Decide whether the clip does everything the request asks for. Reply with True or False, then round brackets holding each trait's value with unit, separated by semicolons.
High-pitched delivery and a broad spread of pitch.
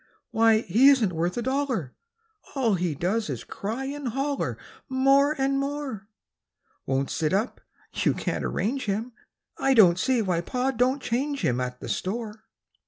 True (230 Hz; 6.0 semitones)